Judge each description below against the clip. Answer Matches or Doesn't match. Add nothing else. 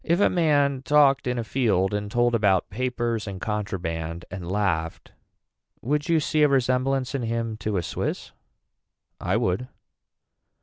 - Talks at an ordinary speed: Matches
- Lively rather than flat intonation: Matches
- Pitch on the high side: Doesn't match